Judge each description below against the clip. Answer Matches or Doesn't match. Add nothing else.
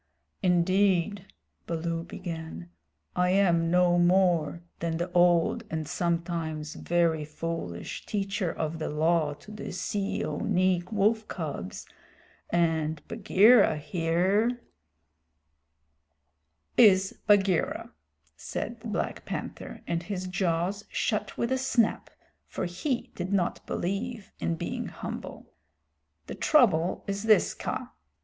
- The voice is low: Doesn't match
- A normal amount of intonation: Matches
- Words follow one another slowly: Matches